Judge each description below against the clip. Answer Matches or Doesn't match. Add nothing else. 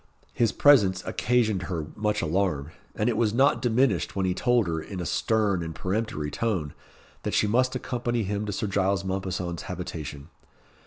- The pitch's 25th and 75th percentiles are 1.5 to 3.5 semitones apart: Doesn't match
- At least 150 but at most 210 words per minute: Matches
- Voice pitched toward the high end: Doesn't match